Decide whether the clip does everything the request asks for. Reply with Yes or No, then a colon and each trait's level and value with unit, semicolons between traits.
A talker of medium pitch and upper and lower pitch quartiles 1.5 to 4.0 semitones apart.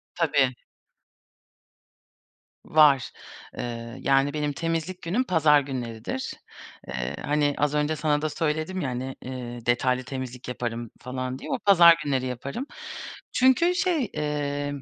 Yes: medium, 145 Hz; average, 3.7 semitones